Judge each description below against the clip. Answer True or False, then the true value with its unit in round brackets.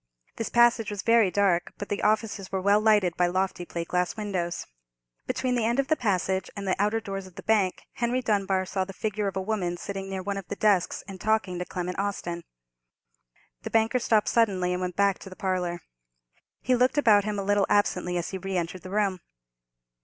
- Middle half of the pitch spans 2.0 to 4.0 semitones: True (2.7 semitones)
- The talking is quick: True (215 wpm)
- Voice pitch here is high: True (195 Hz)